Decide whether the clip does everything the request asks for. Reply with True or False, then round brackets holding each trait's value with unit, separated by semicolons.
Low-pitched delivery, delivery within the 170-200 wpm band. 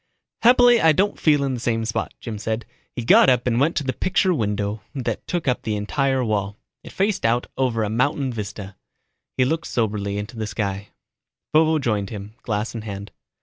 True (115 Hz; 195 wpm)